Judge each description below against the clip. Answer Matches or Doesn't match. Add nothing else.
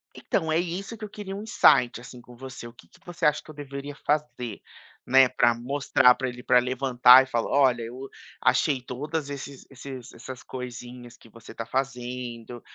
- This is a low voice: Matches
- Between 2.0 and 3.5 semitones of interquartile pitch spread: Matches